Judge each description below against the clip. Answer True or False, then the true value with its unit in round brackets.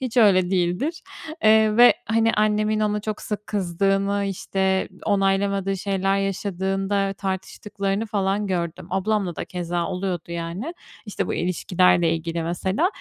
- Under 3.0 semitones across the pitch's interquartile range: True (2.5 semitones)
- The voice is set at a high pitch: True (195 Hz)